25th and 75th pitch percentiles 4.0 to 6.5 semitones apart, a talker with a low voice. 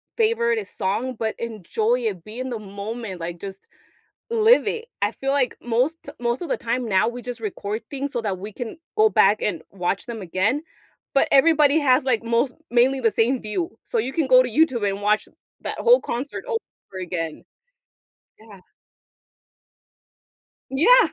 No: average, 5.1 semitones; high, 240 Hz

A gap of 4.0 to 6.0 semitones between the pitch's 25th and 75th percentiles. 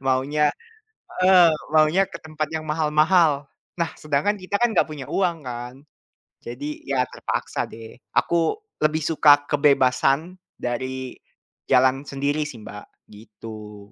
No: average, 3.5 semitones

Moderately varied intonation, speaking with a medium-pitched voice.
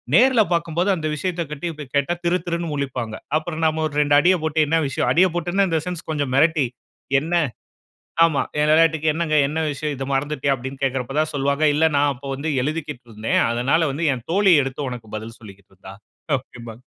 Yes: average, 3.8 semitones; medium, 150 Hz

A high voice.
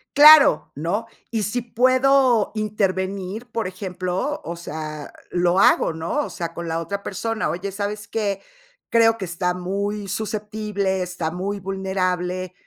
Yes: high, 195 Hz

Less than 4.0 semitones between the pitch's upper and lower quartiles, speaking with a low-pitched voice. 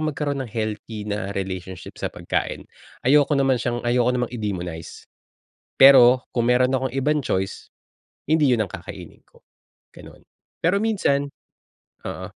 No: average, 4.7 semitones; low, 125 Hz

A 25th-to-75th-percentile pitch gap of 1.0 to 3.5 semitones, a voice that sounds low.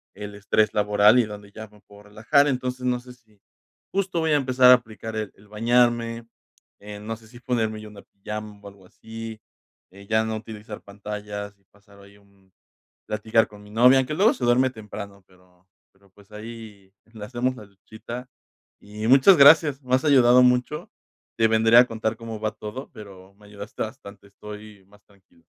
Yes: average, 3.0 semitones; low, 110 Hz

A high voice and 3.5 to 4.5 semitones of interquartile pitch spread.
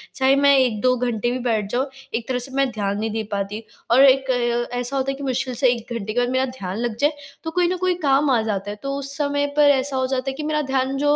No: very high, 255 Hz; average, 2.9 semitones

